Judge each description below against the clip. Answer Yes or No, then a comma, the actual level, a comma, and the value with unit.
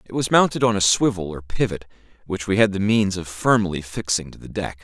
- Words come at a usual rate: No, fast, 235 wpm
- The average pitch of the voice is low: Yes, low, 100 Hz